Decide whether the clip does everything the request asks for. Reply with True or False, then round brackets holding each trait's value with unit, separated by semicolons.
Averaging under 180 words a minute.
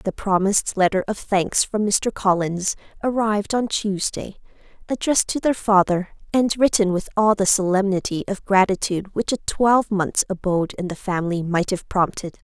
True (160 wpm)